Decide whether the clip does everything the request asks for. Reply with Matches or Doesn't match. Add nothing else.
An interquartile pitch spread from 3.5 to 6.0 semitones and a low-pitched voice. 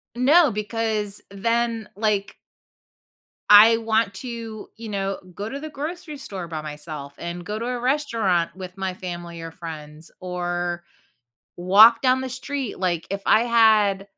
Doesn't match